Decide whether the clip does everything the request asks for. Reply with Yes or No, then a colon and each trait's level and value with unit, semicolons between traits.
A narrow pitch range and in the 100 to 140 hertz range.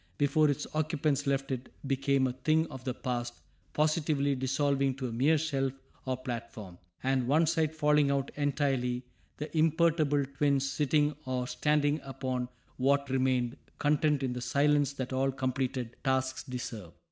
Yes: narrow, 2.3 semitones; low, 135 Hz